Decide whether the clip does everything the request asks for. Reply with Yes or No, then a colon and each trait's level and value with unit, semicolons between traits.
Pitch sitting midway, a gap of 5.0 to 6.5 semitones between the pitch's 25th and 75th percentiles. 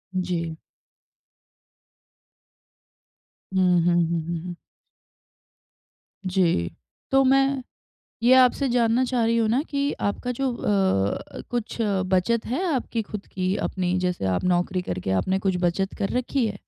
No: high, 195 Hz; wide, 5.4 semitones